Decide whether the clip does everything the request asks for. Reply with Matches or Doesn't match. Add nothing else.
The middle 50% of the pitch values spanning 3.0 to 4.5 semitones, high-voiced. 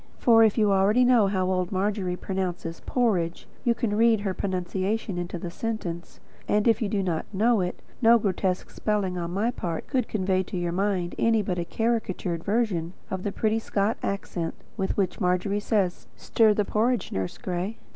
Matches